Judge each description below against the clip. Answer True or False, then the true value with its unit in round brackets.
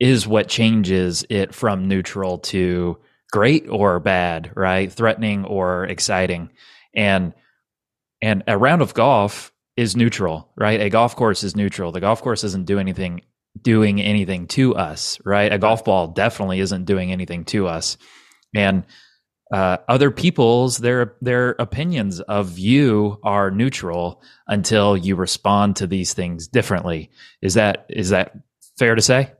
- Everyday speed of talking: True (150 wpm)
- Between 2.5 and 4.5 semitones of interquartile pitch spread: True (3.5 semitones)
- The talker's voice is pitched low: True (100 Hz)